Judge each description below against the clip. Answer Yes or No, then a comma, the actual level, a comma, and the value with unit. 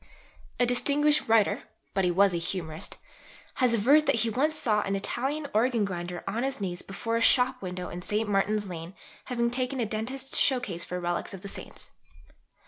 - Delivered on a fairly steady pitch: No, average, 5.1 semitones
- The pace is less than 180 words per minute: No, average, 185 wpm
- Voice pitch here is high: Yes, high, 215 Hz